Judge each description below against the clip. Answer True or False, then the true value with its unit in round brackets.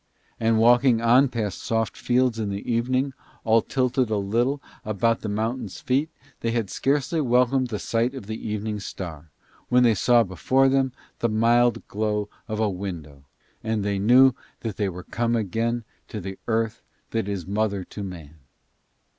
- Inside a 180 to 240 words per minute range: False (165 wpm)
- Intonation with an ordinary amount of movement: True (3.1 semitones)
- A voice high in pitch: False (115 Hz)